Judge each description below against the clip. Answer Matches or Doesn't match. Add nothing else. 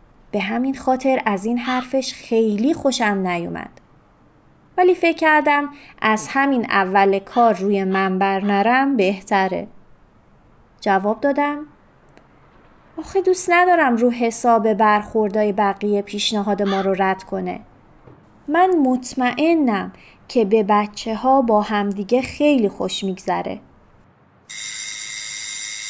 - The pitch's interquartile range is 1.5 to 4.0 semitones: Doesn't match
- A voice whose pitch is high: Matches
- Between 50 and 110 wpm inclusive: Matches